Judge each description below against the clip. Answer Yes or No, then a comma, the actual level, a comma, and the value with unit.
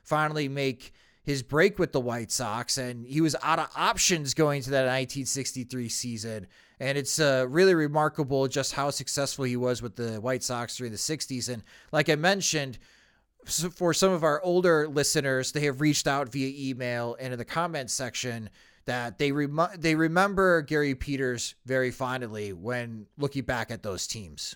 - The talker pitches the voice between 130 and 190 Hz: Yes, low, 135 Hz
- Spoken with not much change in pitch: No, average, 3.7 semitones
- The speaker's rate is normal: Yes, average, 180 wpm